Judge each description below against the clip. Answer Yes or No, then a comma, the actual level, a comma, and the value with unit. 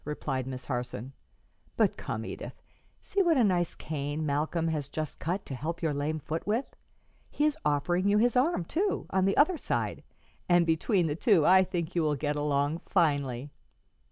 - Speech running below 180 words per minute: No, average, 185 wpm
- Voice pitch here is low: No, medium, 160 Hz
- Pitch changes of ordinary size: Yes, average, 4.6 semitones